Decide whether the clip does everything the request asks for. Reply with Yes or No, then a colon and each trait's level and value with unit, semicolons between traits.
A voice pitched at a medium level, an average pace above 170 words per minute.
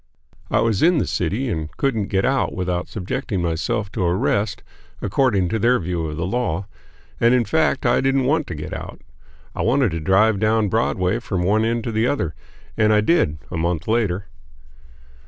No: low, 105 Hz; average, 190 wpm